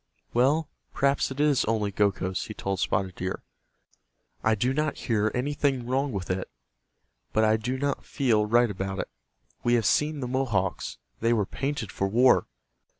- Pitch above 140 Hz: No, low, 120 Hz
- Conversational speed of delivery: Yes, average, 165 wpm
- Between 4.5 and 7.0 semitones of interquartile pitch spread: Yes, average, 4.8 semitones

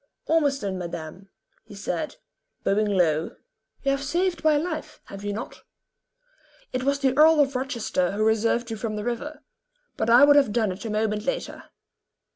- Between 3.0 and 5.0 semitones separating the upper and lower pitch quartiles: No, wide, 5.6 semitones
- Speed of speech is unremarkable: Yes, average, 170 wpm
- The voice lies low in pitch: No, high, 235 Hz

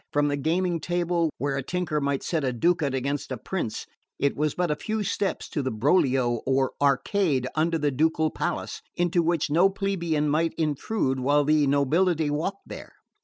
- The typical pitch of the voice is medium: Yes, medium, 150 Hz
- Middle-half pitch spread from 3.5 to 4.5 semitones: Yes, average, 3.8 semitones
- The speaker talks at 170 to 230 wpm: Yes, average, 180 wpm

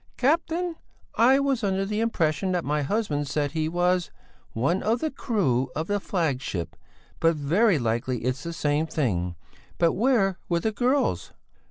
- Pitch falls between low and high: Yes, medium, 175 Hz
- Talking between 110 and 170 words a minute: Yes, average, 160 wpm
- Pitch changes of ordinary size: No, wide, 7.4 semitones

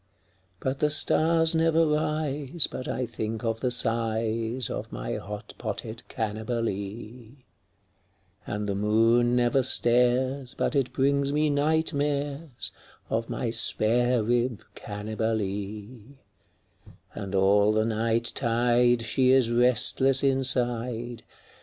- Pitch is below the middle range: Yes, low, 120 Hz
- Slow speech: Yes, slow, 115 wpm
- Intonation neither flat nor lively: Yes, average, 3.3 semitones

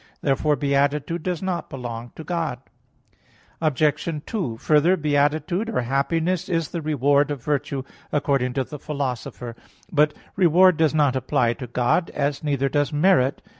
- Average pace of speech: Yes, average, 160 wpm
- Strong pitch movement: No, average, 3.2 semitones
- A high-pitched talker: No, medium, 145 Hz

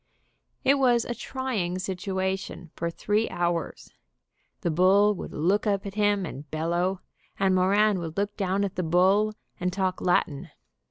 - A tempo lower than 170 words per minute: Yes, average, 155 wpm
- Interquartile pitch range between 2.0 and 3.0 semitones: Yes, average, 2.7 semitones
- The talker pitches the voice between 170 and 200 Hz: Yes, high, 190 Hz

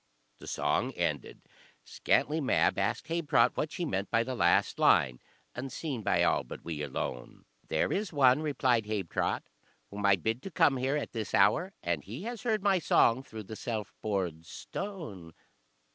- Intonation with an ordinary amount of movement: No, wide, 7.6 semitones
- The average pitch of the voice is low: Yes, low, 120 Hz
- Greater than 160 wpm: Yes, average, 170 wpm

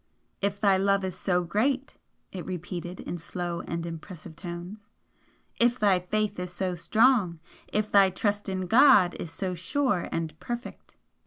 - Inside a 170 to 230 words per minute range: No, average, 155 wpm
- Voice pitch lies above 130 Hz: Yes, medium, 185 Hz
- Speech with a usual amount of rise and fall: Yes, average, 3.2 semitones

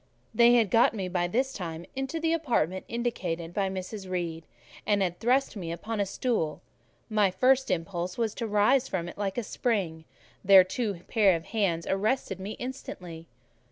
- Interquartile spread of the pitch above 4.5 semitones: Yes, average, 4.9 semitones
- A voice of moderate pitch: No, high, 195 Hz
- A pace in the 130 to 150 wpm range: No, average, 170 wpm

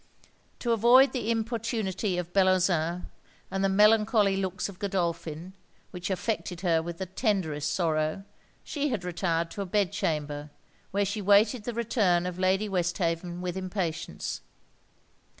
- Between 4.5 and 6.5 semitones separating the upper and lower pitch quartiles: No, average, 3.4 semitones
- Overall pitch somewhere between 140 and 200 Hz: Yes, high, 190 Hz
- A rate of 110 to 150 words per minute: Yes, average, 140 wpm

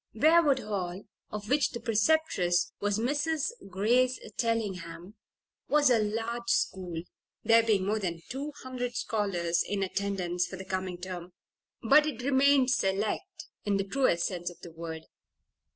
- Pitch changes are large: Yes, wide, 5.7 semitones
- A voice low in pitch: No, high, 210 Hz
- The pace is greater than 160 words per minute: No, average, 145 wpm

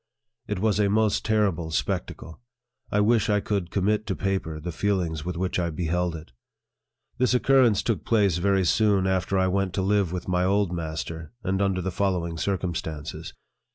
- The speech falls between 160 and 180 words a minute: Yes, average, 175 wpm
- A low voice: Yes, very low, 95 Hz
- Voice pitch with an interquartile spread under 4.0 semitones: Yes, average, 3.1 semitones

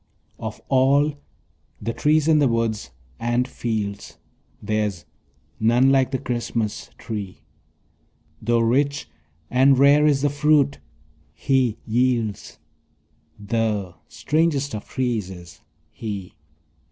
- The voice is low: Yes, low, 120 Hz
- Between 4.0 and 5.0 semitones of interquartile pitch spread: Yes, average, 4.5 semitones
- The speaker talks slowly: Yes, slow, 105 wpm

